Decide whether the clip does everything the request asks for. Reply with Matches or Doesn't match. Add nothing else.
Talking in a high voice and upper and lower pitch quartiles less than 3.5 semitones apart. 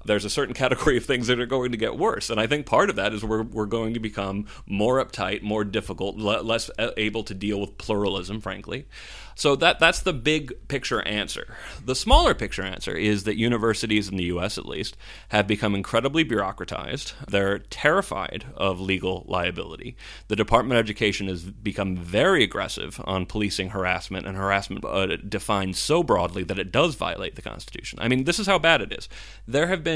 Doesn't match